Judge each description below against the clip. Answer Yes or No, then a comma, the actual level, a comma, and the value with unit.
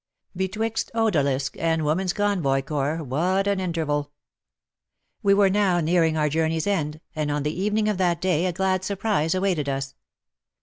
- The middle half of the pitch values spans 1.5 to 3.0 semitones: No, average, 4.3 semitones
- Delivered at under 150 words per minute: No, average, 160 wpm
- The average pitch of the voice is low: No, medium, 170 Hz